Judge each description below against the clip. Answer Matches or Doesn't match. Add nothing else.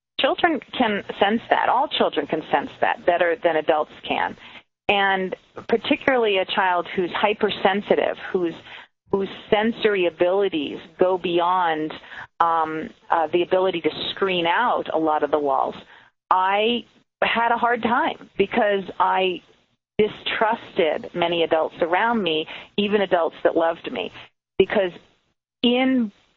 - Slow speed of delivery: Matches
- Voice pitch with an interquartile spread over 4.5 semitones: Matches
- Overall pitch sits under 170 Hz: Doesn't match